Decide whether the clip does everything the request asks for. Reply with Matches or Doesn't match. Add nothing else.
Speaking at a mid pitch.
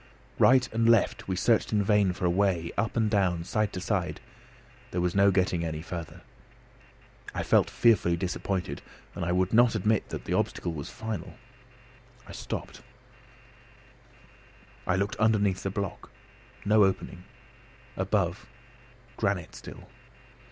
Doesn't match